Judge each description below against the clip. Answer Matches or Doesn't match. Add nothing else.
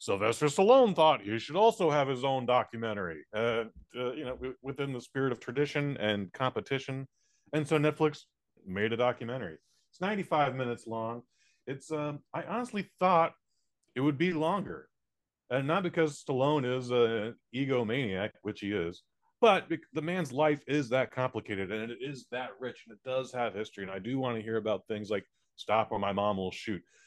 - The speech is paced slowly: Doesn't match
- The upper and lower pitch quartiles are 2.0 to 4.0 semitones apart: Doesn't match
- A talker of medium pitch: Doesn't match